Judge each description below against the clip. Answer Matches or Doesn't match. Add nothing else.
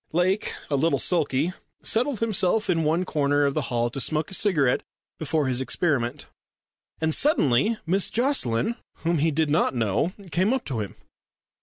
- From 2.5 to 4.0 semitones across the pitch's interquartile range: Doesn't match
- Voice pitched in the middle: Matches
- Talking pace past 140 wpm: Matches